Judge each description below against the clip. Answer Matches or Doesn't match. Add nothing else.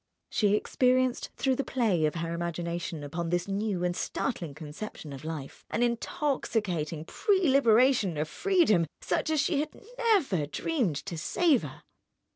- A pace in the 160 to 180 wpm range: Doesn't match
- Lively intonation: Matches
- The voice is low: Doesn't match